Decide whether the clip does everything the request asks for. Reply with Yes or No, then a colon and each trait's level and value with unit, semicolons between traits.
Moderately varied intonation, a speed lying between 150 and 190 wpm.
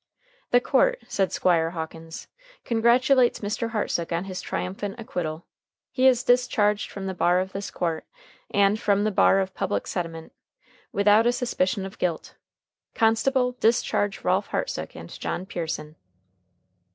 No: average, 4.5 semitones; average, 140 wpm